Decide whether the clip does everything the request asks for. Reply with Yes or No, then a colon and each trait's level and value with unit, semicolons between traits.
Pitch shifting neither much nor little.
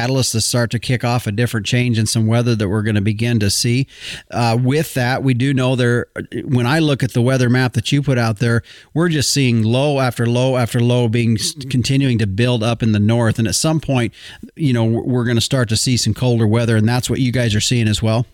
No: narrow, 2.1 semitones